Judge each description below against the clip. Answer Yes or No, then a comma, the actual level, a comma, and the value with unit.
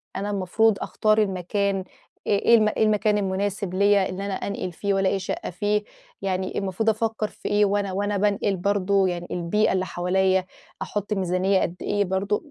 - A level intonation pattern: Yes, narrow, 1.6 semitones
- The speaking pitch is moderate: No, high, 200 Hz